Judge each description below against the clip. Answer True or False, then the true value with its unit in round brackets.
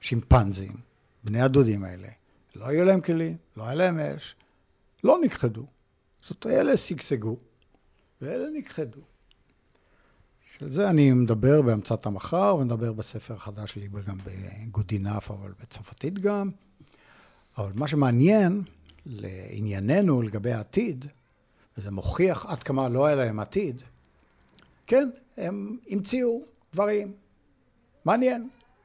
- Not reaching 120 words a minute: True (110 wpm)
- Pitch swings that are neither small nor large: False (9.0 semitones)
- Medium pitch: False (130 Hz)